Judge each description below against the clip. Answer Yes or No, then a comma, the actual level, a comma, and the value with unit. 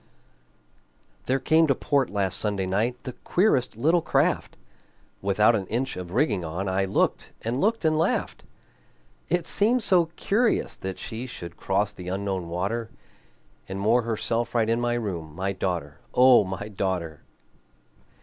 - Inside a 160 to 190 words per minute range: No, average, 150 wpm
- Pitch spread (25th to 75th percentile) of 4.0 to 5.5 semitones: Yes, average, 5.2 semitones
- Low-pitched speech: Yes, low, 110 Hz